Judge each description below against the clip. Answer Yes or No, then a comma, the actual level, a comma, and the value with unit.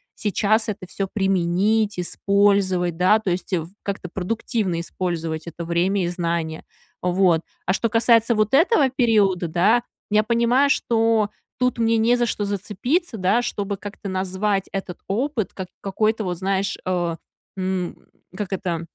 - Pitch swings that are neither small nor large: Yes, average, 3.6 semitones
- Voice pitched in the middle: No, high, 200 Hz